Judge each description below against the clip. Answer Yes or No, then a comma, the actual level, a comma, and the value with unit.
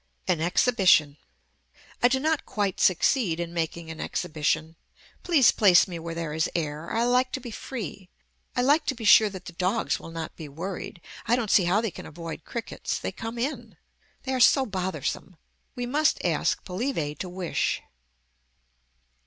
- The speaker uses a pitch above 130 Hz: Yes, high, 190 Hz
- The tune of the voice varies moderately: No, wide, 6.5 semitones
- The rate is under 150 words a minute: No, average, 175 wpm